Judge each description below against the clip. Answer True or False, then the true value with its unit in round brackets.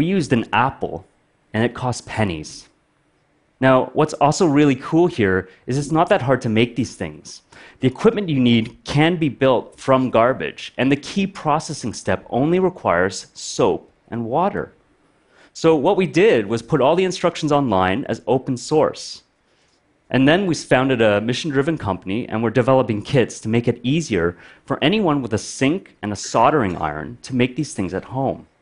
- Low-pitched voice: True (130 Hz)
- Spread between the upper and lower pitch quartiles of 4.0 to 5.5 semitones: True (5.2 semitones)